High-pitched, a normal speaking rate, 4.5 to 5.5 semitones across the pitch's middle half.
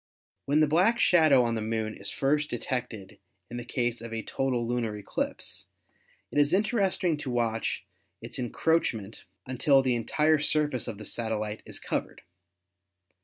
No: low, 125 Hz; average, 155 wpm; average, 5.0 semitones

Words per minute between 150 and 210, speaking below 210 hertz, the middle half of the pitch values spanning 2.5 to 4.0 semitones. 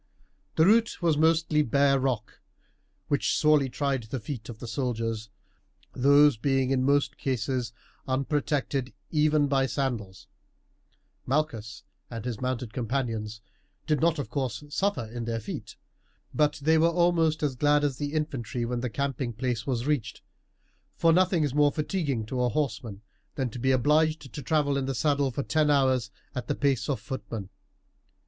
Yes: average, 160 wpm; low, 135 Hz; average, 3.7 semitones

